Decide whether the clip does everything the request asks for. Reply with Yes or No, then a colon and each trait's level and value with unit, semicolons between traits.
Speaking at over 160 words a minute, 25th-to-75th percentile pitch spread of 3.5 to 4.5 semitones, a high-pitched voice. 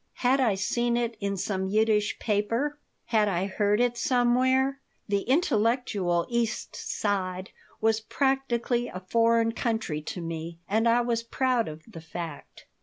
No: average, 145 wpm; average, 3.8 semitones; high, 225 Hz